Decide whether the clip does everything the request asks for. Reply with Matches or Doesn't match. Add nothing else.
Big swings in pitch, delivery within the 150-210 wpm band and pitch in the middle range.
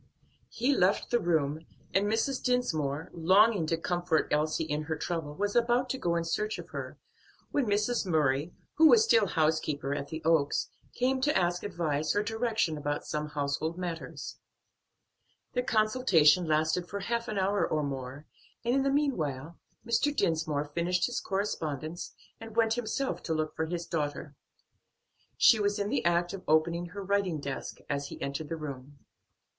Matches